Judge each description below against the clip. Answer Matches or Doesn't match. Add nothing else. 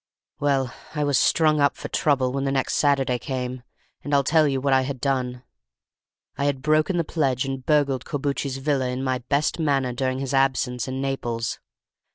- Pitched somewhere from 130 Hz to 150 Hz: Matches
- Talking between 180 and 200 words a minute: Matches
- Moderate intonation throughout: Doesn't match